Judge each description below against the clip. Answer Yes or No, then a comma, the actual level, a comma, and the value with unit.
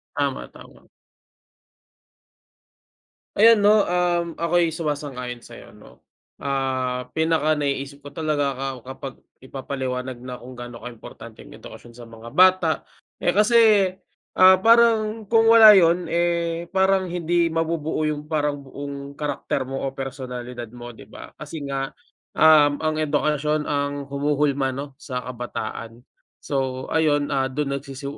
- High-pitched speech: No, medium, 145 Hz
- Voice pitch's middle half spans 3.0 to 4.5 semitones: Yes, average, 4.2 semitones